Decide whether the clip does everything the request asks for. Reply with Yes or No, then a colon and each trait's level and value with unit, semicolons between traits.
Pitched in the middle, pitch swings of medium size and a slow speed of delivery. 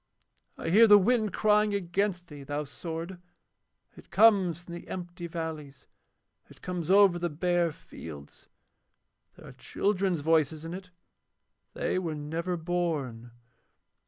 Yes: medium, 175 Hz; average, 3.0 semitones; slow, 130 wpm